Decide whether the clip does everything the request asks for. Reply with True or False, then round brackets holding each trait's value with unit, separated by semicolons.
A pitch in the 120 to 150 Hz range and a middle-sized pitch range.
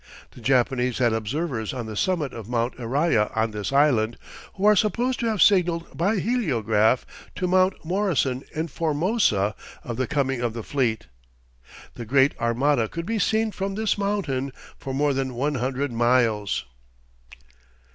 False (135 Hz; 7.4 semitones)